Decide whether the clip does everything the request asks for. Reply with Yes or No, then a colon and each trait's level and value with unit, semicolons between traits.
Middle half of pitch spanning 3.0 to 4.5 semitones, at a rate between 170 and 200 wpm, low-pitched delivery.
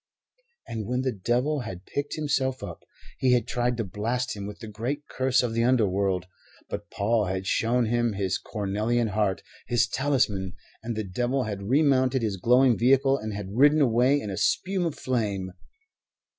Yes: average, 4.0 semitones; average, 175 wpm; low, 120 Hz